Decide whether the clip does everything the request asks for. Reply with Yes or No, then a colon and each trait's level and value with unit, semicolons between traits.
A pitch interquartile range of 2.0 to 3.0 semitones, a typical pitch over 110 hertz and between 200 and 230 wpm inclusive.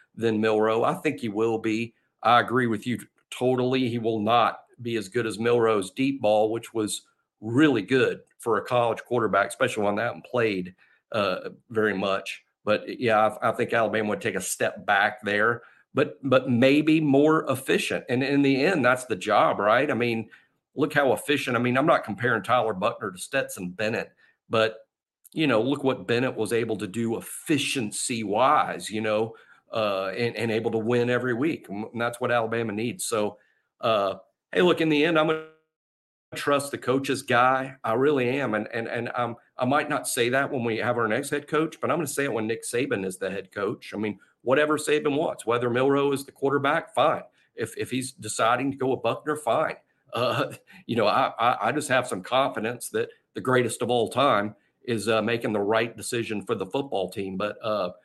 No: average, 3.4 semitones; low, 120 Hz; fast, 205 wpm